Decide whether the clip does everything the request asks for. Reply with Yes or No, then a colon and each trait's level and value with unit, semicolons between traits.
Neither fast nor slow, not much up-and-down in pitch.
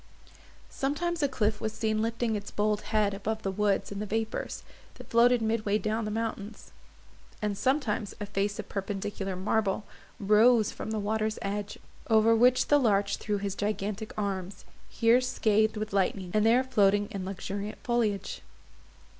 Yes: average, 165 wpm; narrow, 1.9 semitones